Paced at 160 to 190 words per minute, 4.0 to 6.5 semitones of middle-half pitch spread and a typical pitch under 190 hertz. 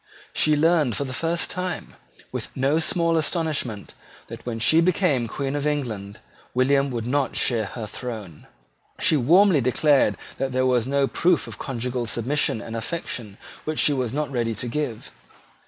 Yes: average, 165 wpm; average, 4.5 semitones; low, 135 Hz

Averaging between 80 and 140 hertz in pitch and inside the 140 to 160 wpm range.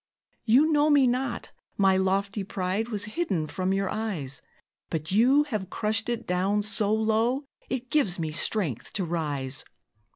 No: high, 205 Hz; average, 155 wpm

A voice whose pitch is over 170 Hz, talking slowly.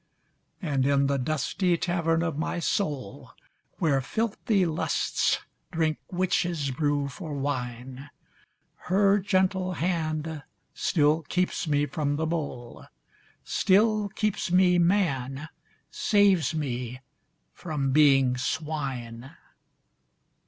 No: medium, 155 Hz; slow, 100 wpm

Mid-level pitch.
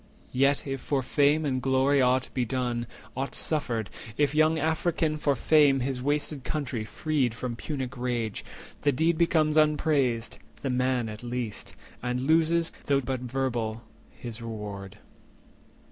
No: low, 130 Hz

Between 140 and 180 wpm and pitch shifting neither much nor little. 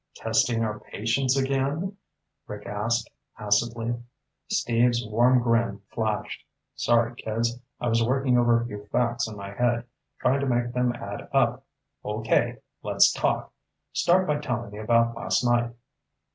No: average, 145 wpm; narrow, 1.6 semitones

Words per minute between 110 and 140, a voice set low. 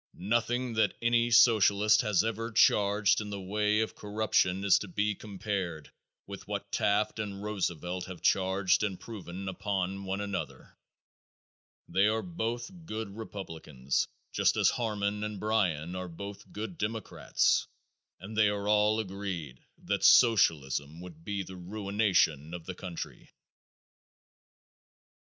Yes: slow, 135 wpm; low, 100 Hz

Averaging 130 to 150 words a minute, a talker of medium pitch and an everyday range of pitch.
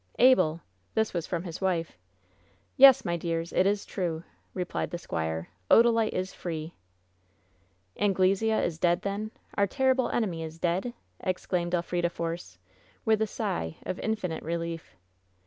No: average, 160 wpm; medium, 175 Hz; average, 3.8 semitones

